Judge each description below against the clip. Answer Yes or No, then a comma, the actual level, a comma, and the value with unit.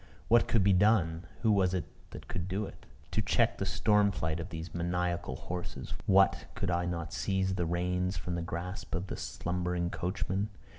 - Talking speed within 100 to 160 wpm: No, average, 190 wpm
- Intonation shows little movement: Yes, narrow, 1.9 semitones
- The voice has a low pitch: Yes, very low, 90 Hz